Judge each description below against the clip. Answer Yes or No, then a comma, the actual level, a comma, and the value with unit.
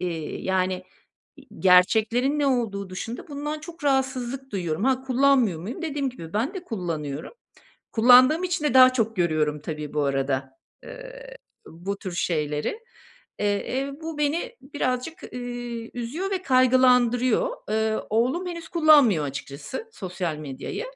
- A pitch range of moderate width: No, wide, 7.8 semitones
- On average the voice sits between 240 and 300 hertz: Yes, high, 245 Hz